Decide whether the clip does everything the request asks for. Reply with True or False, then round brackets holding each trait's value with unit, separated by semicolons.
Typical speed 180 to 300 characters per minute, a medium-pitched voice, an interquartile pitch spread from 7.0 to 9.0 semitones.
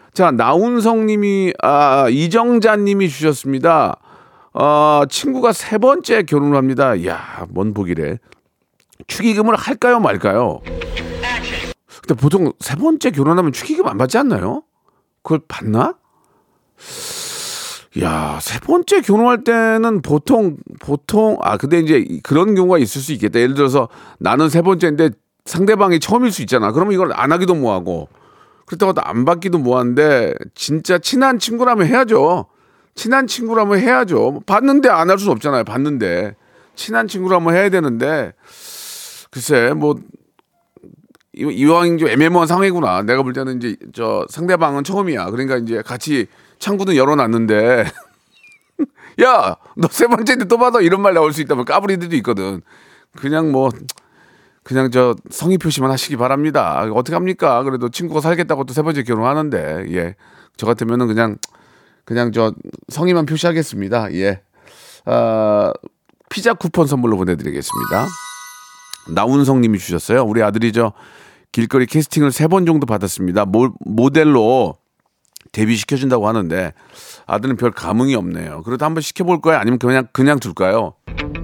False (310 characters per minute; 155 Hz; 8.4 semitones)